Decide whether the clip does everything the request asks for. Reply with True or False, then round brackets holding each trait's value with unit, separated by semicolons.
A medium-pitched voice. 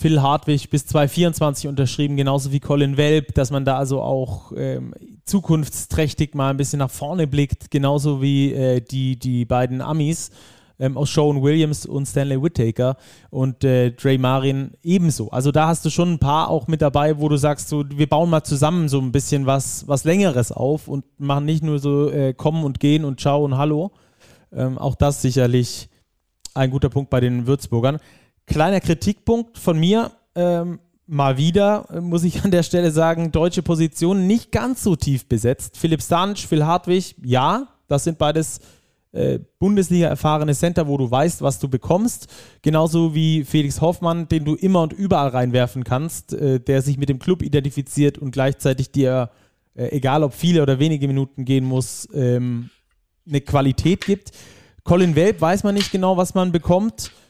True (145 Hz)